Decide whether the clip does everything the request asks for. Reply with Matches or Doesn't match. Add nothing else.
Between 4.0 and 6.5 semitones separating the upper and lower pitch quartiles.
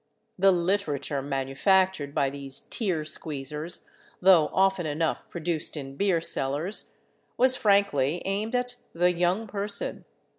Matches